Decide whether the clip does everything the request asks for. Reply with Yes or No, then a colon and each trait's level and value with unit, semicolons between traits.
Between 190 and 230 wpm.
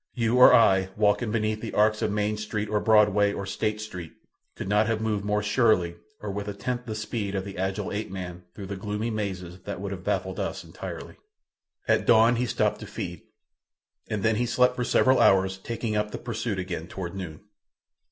Yes: fast, 205 wpm